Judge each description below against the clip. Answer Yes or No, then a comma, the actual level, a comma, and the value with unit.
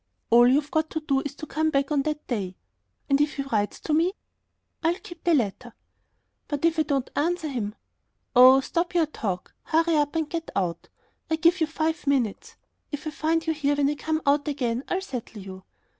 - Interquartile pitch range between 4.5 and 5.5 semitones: No, average, 3.7 semitones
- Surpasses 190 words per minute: Yes, fast, 205 wpm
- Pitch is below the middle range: No, very high, 290 Hz